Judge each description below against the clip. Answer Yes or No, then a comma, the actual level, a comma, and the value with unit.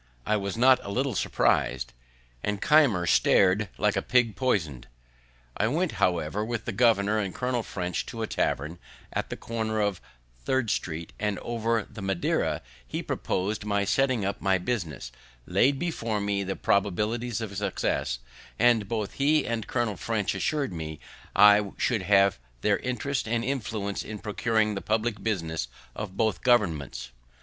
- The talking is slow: No, average, 160 wpm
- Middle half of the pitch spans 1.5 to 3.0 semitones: No, average, 3.5 semitones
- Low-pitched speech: Yes, low, 105 Hz